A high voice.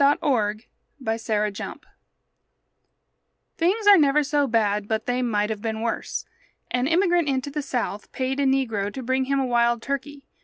Yes: very high, 255 Hz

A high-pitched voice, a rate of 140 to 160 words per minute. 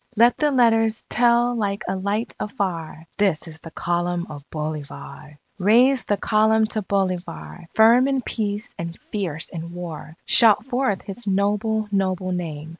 Yes: high, 200 Hz; average, 150 wpm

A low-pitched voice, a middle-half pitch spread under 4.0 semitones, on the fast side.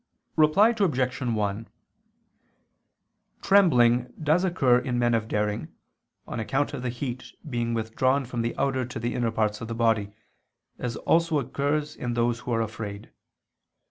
No: low, 120 Hz; average, 3.5 semitones; average, 150 wpm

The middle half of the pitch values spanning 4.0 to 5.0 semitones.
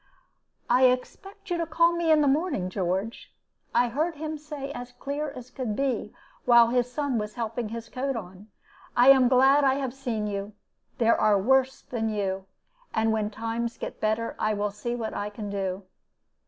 Yes: average, 4.3 semitones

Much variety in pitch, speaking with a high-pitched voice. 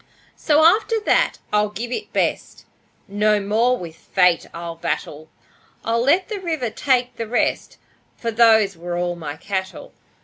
Yes: wide, 5.8 semitones; high, 220 Hz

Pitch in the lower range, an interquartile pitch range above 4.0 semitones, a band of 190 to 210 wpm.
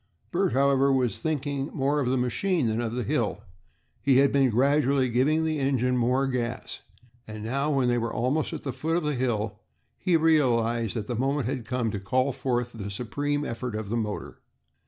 No: low, 130 Hz; average, 3.1 semitones; average, 200 wpm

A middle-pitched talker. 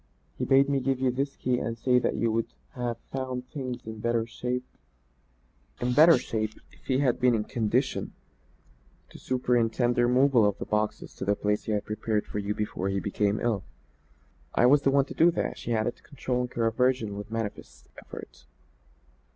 No: low, 120 Hz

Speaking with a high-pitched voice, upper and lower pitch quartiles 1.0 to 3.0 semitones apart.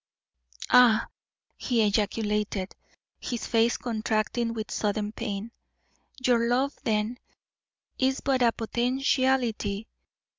Yes: high, 230 Hz; narrow, 2.6 semitones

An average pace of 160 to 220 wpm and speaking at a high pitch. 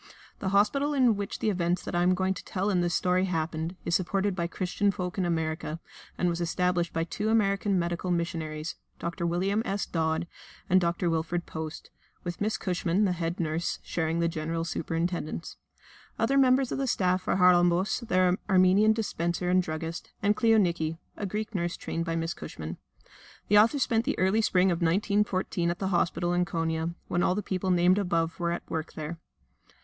No: average, 185 wpm; medium, 180 Hz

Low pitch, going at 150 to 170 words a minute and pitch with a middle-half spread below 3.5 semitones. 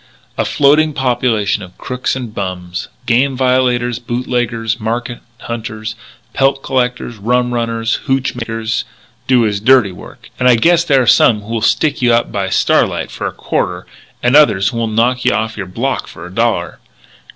Yes: low, 120 Hz; average, 165 wpm; narrow, 2.6 semitones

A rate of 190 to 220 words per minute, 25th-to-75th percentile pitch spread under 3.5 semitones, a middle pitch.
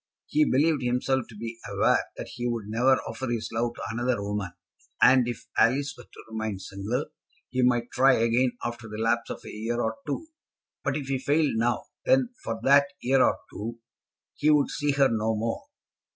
No: average, 195 wpm; average, 2.9 semitones; low, 120 Hz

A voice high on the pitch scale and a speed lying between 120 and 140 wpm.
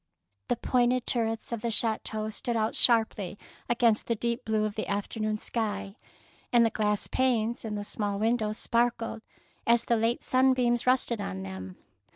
No: high, 225 Hz; average, 165 wpm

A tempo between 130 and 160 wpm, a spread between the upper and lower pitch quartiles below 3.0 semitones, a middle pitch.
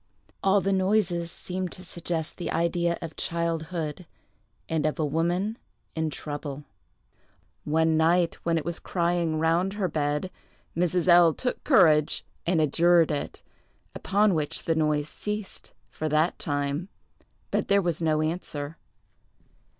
Yes: slow, 135 wpm; narrow, 2.4 semitones; medium, 165 Hz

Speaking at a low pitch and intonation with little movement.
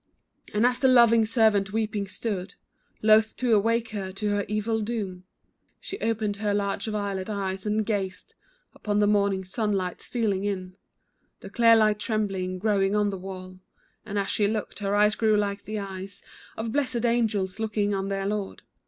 No: high, 205 Hz; narrow, 2.0 semitones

